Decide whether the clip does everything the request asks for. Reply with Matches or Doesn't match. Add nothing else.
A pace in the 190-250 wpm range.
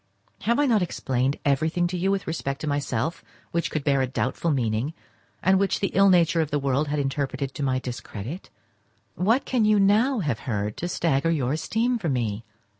Matches